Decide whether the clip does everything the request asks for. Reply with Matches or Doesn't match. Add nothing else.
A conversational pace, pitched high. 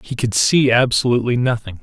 Doesn't match